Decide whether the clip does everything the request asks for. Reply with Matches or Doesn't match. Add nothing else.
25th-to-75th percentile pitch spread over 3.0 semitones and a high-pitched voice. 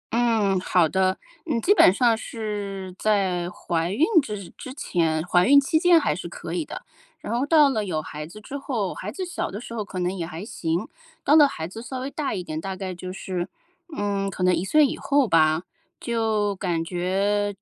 Matches